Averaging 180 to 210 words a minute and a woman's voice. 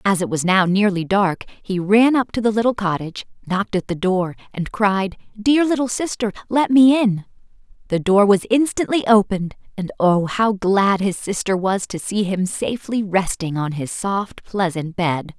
Yes: average, 185 wpm; female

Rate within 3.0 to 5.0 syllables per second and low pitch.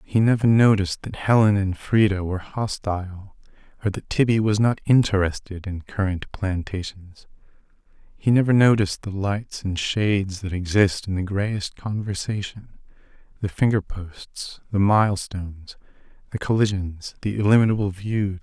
Yes: 4.7 syllables/s; low, 100 Hz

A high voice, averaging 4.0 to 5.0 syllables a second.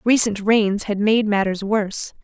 Yes: high, 210 Hz; 4.4 syllables/s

